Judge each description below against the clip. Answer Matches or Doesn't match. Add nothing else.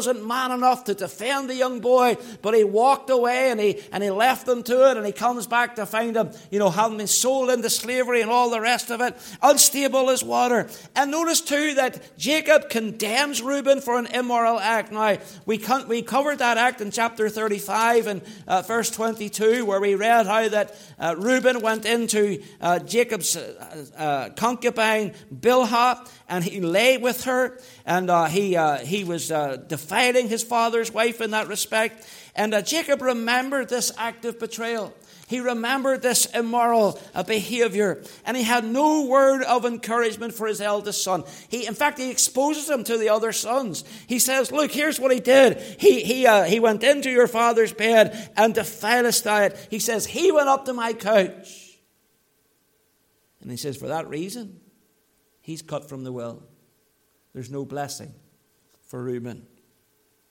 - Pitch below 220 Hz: Doesn't match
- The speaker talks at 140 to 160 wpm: Doesn't match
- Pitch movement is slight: Doesn't match